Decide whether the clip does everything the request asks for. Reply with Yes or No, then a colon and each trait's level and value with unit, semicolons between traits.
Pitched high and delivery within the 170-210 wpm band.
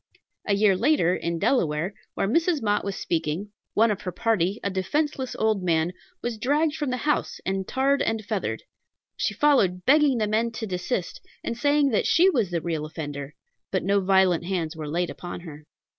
Yes: high, 200 Hz; average, 190 wpm